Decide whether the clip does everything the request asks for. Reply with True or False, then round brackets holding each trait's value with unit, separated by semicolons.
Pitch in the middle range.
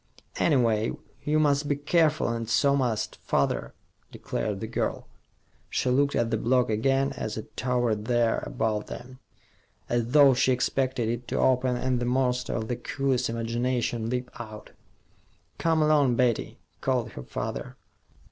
False (125 Hz)